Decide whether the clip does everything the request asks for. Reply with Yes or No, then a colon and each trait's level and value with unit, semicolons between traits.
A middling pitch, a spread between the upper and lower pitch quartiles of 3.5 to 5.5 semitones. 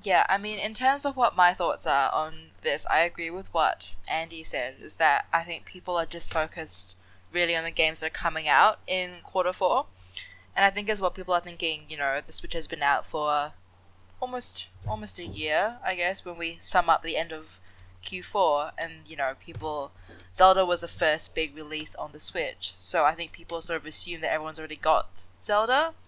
Yes: medium, 165 Hz; average, 4.3 semitones